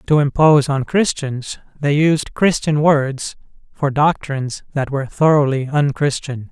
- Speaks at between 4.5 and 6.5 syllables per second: No, 4.3 syllables/s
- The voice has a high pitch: No, medium, 145 Hz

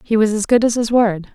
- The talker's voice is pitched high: Yes, high, 220 Hz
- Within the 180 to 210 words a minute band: No, fast, 315 wpm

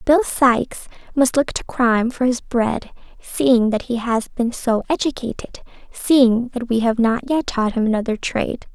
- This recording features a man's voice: No, female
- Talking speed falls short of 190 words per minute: Yes, average, 180 wpm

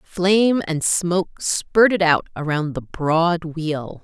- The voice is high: No, medium, 170 Hz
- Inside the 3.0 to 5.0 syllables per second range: Yes, 3.4 syllables/s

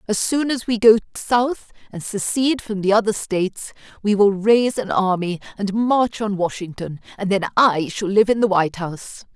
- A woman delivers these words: Yes, female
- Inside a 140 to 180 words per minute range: No, average, 190 wpm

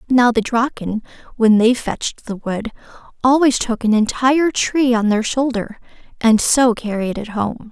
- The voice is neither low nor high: No, high, 235 Hz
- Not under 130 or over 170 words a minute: Yes, average, 165 wpm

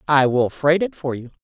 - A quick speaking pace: Yes, fast, 250 wpm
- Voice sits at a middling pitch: Yes, medium, 150 Hz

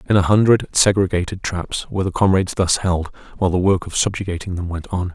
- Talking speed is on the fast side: Yes, fast, 210 wpm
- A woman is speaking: No, male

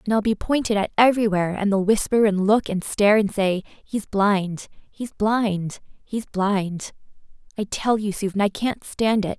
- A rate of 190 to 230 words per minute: No, average, 175 wpm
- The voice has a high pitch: Yes, high, 205 Hz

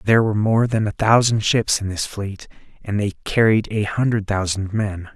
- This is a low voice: Yes, low, 105 Hz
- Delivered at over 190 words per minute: Yes, average, 200 wpm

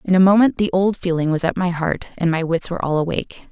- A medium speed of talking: No, fast, 275 wpm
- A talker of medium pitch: Yes, medium, 175 Hz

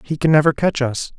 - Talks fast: Yes, fast, 255 wpm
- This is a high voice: No, medium, 145 Hz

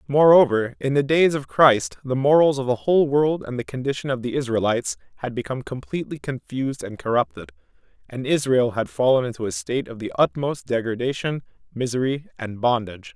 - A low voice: Yes, low, 130 Hz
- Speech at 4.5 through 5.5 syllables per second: No, 5.9 syllables/s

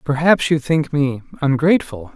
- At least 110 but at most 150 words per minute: Yes, average, 140 wpm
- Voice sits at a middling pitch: Yes, medium, 145 Hz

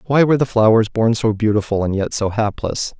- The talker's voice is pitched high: No, low, 110 Hz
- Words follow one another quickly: Yes, fast, 220 wpm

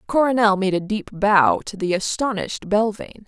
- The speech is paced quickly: No, average, 165 wpm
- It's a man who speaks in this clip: No, female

